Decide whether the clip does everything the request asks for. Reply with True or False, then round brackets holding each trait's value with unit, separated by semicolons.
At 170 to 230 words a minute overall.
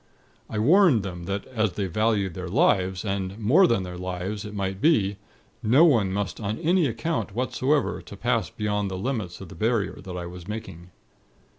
True (180 wpm)